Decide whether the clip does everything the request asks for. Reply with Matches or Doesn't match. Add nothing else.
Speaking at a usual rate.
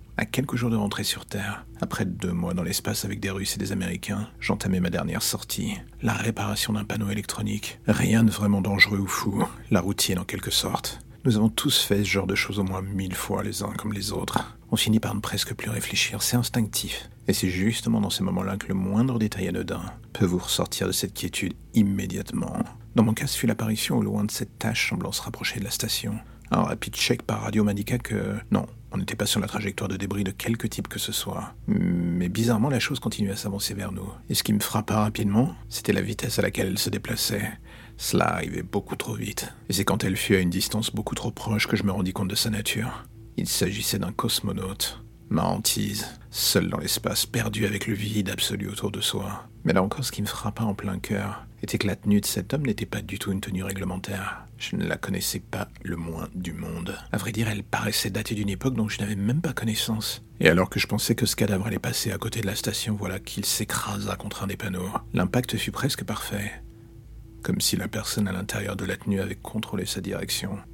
Doesn't match